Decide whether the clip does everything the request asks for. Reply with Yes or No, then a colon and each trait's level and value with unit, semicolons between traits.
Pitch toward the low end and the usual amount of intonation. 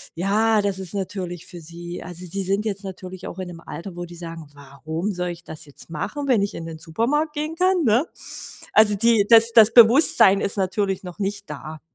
No: high, 190 Hz; average, 4.1 semitones